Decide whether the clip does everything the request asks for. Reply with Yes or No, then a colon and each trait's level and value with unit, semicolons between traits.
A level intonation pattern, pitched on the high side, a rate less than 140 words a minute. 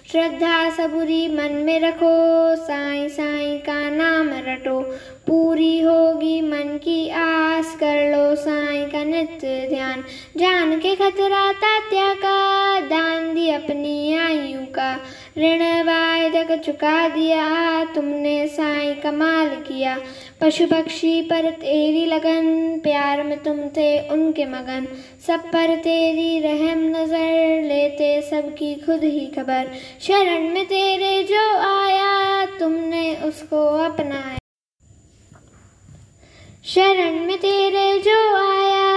Yes: narrow, 2.1 semitones; very high, 320 Hz; slow, 110 wpm